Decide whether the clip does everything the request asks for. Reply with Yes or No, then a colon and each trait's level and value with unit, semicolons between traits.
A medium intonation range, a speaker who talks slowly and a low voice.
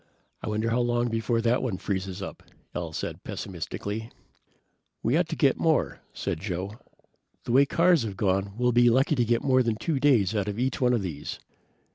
No: average, 4.0 semitones; average, 200 wpm; low, 115 Hz